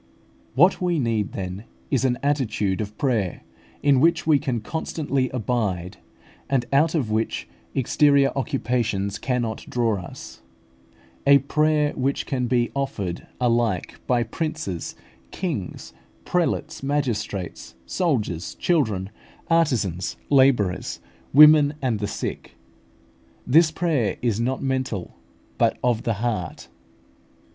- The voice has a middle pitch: No, low, 125 Hz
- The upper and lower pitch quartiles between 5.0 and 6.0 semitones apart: Yes, average, 5.3 semitones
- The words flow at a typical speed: No, slow, 115 wpm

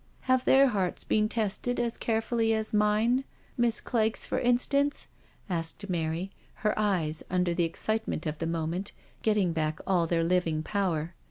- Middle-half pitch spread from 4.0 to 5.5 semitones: Yes, average, 5.1 semitones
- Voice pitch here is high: Yes, high, 200 Hz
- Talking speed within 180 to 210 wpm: No, average, 160 wpm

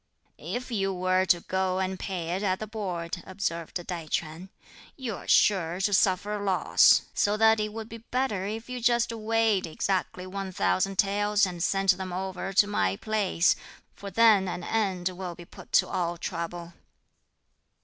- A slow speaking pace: No, average, 170 wpm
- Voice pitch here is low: No, high, 190 Hz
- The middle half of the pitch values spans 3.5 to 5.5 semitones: No, average, 2.8 semitones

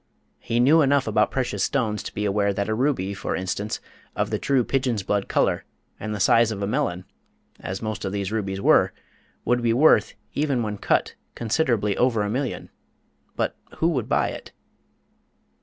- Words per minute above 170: Yes, average, 180 wpm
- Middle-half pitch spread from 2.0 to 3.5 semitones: No, average, 4.1 semitones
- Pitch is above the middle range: No, low, 110 Hz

